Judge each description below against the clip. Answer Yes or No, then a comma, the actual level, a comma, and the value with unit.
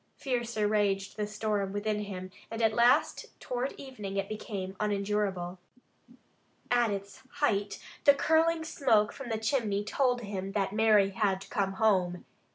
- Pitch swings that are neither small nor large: Yes, average, 3.2 semitones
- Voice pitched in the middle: No, high, 210 Hz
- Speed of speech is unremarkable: Yes, average, 145 wpm